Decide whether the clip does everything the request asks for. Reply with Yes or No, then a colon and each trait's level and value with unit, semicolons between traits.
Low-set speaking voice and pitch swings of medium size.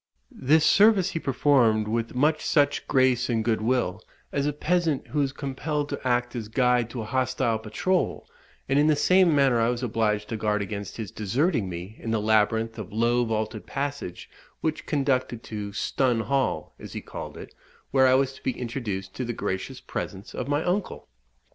Yes: low, 125 Hz; average, 4.4 semitones